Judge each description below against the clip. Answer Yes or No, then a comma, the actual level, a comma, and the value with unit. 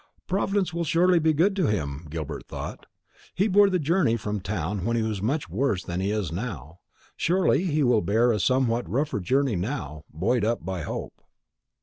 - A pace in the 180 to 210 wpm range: Yes, average, 190 wpm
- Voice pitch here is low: Yes, low, 115 Hz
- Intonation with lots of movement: Yes, wide, 8.8 semitones